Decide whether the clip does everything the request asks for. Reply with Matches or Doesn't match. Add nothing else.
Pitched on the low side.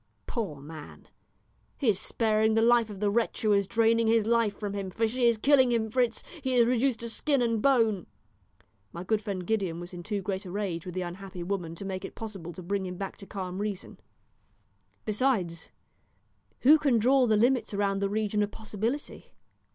Doesn't match